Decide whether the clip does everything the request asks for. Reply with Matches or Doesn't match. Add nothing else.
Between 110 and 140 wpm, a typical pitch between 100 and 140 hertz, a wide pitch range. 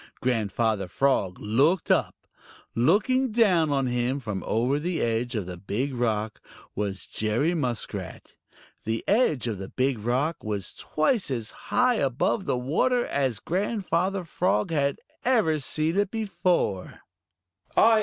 Matches